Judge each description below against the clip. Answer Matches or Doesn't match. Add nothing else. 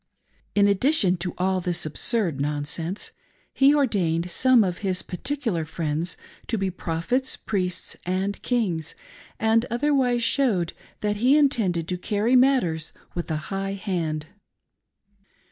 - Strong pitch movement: Matches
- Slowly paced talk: Matches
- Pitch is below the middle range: Doesn't match